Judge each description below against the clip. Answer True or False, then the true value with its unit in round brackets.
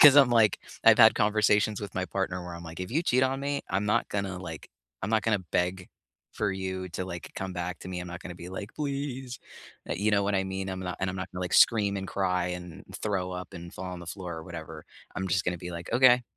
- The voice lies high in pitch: False (95 Hz)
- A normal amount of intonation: True (3.0 semitones)